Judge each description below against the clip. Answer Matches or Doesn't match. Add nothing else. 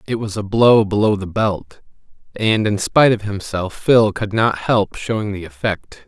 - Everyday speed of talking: Matches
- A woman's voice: Doesn't match